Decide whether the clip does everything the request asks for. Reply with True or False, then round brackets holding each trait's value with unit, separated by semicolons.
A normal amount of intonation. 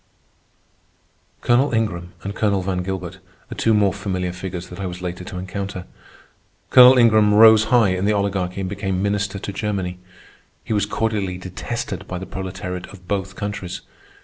False (2.3 semitones)